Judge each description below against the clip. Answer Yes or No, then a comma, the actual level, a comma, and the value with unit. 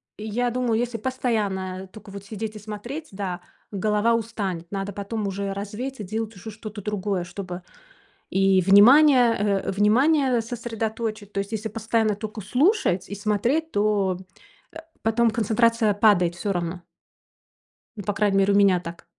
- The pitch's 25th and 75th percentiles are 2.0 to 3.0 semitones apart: Yes, average, 2.7 semitones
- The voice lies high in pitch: Yes, high, 210 Hz